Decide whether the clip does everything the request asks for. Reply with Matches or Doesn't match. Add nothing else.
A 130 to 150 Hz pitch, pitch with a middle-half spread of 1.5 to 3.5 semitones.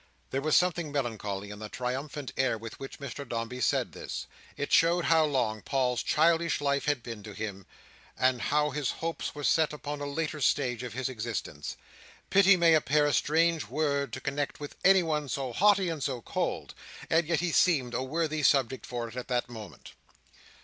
Doesn't match